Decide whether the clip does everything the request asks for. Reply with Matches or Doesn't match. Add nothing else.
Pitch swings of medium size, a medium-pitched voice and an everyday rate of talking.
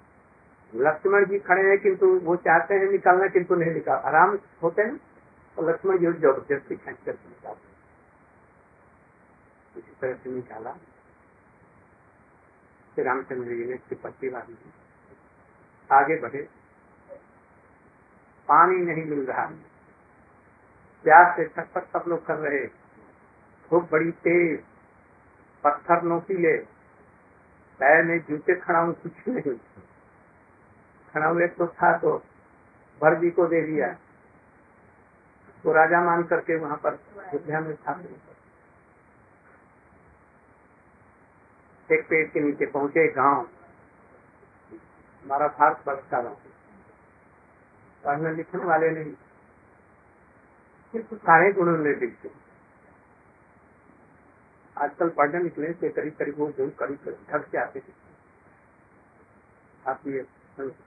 Doesn't match